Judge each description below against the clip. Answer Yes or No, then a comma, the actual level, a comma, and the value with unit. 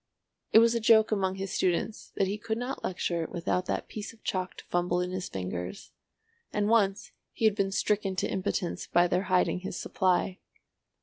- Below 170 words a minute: No, average, 190 wpm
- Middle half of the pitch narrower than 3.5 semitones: Yes, average, 2.9 semitones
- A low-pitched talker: No, high, 190 Hz